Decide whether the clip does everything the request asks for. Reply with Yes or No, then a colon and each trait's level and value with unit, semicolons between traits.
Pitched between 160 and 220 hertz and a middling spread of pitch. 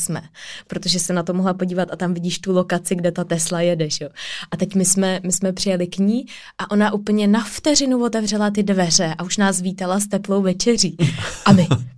No: medium, 185 Hz; narrow, 2.3 semitones